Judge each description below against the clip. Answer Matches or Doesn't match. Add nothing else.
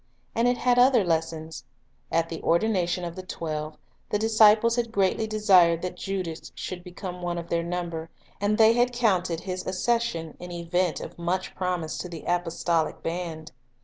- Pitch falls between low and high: Matches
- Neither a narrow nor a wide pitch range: Matches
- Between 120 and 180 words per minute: Matches